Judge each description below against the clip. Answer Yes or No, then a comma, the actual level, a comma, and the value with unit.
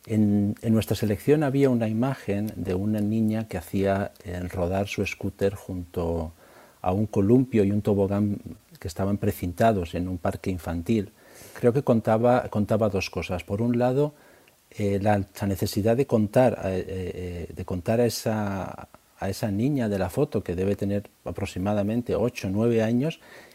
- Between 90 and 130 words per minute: No, average, 165 wpm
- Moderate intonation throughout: Yes, average, 3.0 semitones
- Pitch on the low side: Yes, low, 105 Hz